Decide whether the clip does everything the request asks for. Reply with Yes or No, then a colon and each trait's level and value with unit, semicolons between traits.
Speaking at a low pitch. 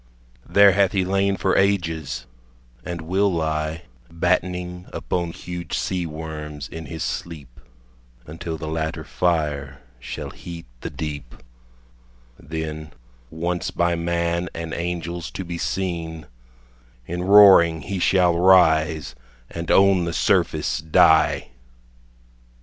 Yes: very low, 85 Hz